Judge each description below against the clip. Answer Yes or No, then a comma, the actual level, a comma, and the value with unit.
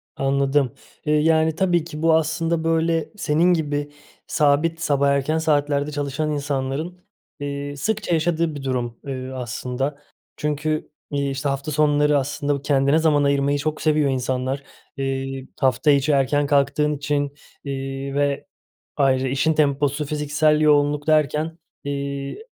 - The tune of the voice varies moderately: No, narrow, 1.9 semitones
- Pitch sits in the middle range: Yes, medium, 145 Hz